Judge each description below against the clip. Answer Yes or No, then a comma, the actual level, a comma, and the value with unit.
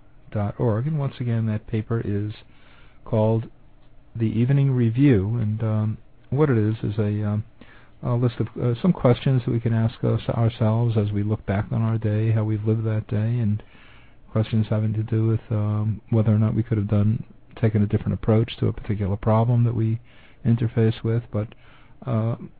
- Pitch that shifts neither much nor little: No, narrow, 1.6 semitones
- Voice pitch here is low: Yes, low, 110 Hz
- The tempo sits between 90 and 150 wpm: No, average, 190 wpm